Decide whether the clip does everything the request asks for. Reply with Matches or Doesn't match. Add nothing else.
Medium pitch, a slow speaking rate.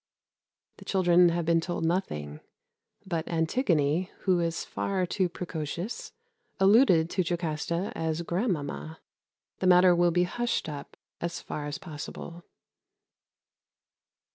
Matches